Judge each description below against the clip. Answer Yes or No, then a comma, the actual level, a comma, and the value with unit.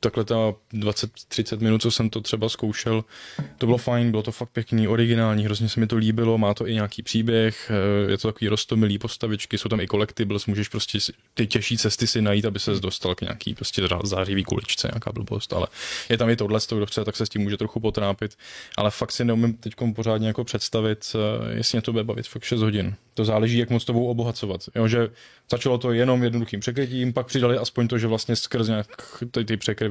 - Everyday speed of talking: No, fast, 210 wpm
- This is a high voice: No, low, 110 Hz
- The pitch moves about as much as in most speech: No, narrow, 1.8 semitones